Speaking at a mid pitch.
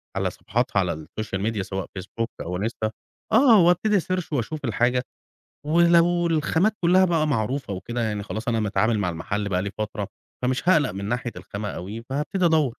No: low, 120 Hz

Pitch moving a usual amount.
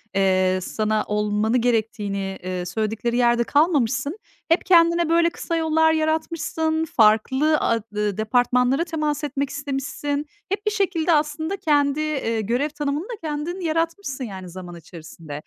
No: wide, 6.8 semitones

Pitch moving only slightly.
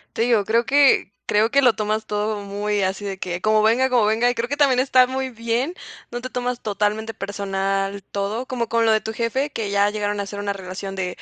No: average, 3.2 semitones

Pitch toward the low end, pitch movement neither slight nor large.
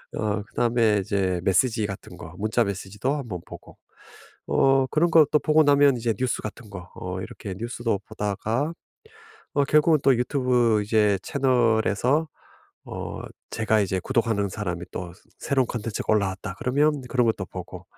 Yes: low, 115 Hz; average, 4.6 semitones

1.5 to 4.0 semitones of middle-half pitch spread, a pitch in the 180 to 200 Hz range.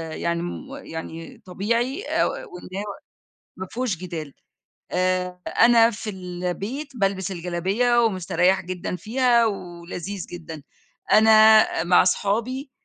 No: average, 4.5 semitones; high, 190 Hz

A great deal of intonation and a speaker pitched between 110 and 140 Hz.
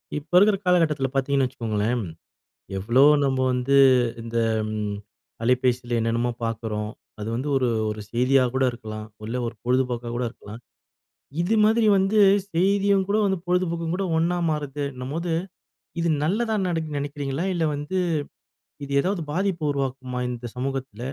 Yes: wide, 5.9 semitones; low, 135 Hz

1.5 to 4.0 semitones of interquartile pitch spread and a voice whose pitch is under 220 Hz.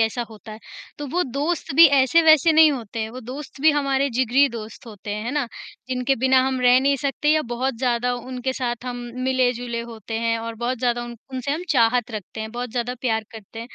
No: average, 2.8 semitones; very high, 250 Hz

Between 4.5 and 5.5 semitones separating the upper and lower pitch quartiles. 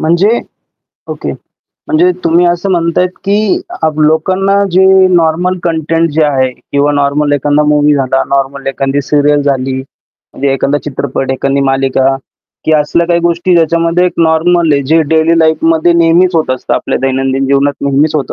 No: average, 3.5 semitones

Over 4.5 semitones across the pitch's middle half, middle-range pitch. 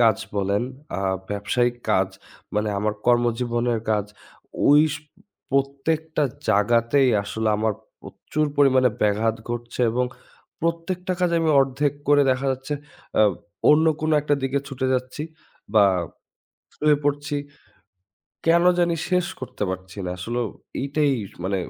No: average, 5.0 semitones; low, 130 Hz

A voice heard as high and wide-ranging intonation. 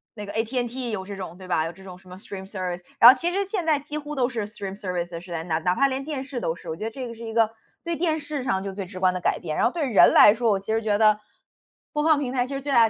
Yes: high, 220 Hz; wide, 6.1 semitones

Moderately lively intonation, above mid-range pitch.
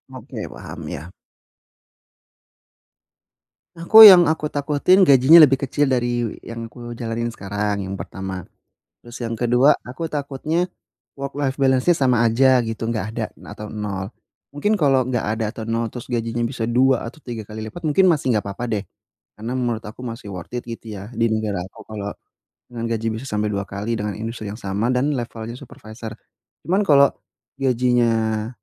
No: average, 3.5 semitones; low, 115 Hz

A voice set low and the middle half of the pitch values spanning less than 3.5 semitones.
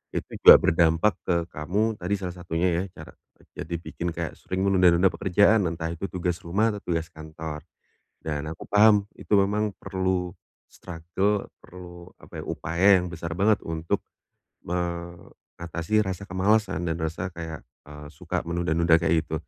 Yes: very low, 85 Hz; narrow, 2.6 semitones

